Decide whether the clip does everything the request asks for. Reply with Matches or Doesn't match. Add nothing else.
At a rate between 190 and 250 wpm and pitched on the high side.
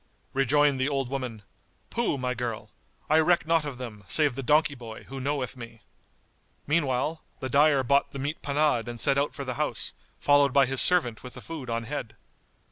Doesn't match